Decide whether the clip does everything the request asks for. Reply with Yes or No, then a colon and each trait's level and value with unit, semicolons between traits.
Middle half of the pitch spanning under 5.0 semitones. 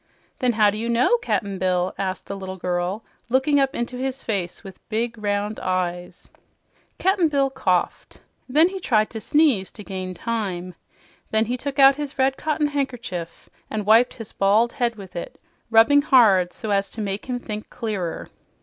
No: average, 5.3 semitones